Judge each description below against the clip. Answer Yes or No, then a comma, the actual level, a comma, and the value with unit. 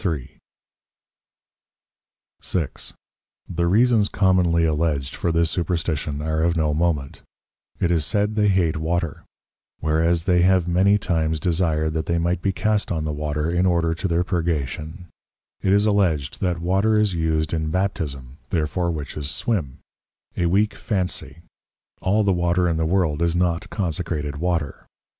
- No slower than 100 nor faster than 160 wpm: Yes, average, 150 wpm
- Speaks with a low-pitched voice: Yes, very low, 85 Hz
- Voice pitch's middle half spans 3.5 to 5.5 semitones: No, average, 2.9 semitones